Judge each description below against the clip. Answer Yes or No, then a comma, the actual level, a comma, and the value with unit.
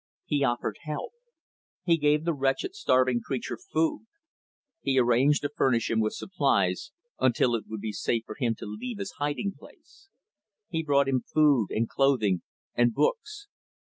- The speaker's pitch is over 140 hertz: No, low, 135 Hz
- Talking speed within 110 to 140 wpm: No, average, 160 wpm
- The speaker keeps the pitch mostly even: No, average, 5.1 semitones